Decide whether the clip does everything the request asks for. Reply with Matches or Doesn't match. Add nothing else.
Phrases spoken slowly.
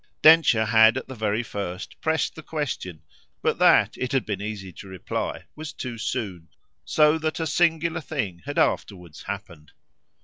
Doesn't match